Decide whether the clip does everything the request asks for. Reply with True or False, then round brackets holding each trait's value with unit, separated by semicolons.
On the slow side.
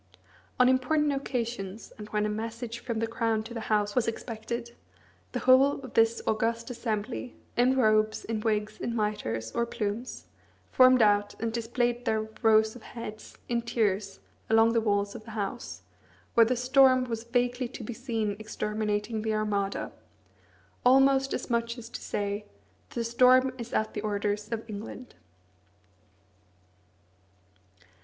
False (150 wpm)